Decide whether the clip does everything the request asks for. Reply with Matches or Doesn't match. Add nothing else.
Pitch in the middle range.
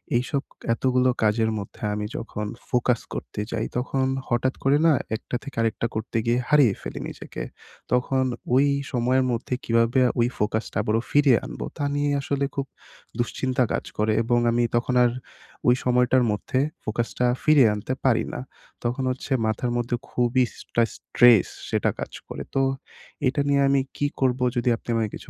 Doesn't match